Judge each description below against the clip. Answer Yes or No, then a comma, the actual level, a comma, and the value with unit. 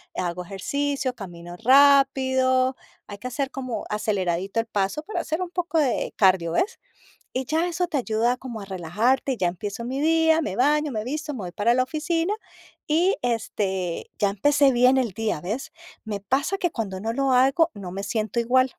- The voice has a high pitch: Yes, very high, 250 Hz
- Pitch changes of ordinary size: No, wide, 5.9 semitones